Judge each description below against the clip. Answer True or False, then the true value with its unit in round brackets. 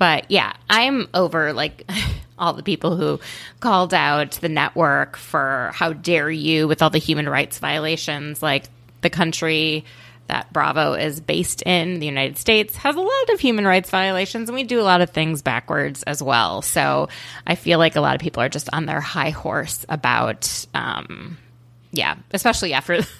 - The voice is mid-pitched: True (160 Hz)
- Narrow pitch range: False (3.8 semitones)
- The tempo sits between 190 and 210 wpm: False (180 wpm)